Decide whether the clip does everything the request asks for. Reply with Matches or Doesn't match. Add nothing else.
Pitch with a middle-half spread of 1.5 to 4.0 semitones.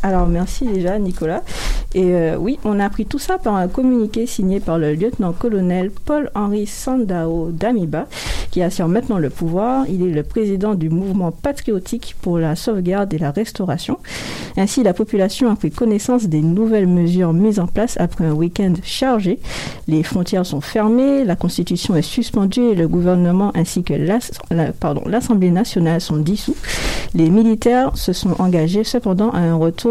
Doesn't match